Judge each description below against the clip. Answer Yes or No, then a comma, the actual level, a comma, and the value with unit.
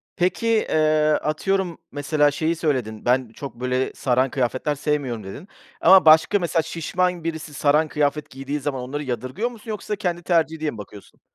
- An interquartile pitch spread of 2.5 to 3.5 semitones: No, average, 4.2 semitones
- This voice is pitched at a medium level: Yes, medium, 150 Hz